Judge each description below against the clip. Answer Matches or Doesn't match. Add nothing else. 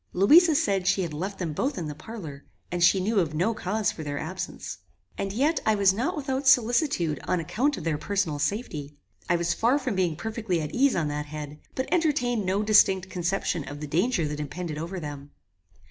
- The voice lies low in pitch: Doesn't match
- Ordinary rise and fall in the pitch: Doesn't match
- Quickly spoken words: Matches